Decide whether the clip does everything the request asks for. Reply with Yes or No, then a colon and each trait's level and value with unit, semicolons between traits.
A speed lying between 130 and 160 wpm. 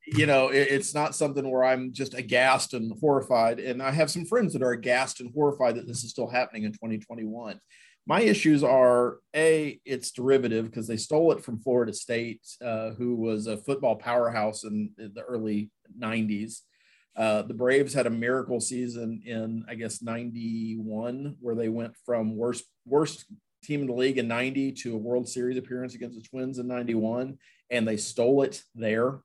No: average, 185 wpm